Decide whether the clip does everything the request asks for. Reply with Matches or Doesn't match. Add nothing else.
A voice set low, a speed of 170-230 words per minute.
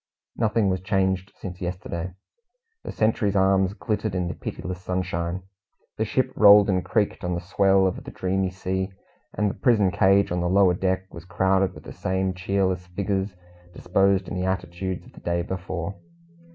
Matches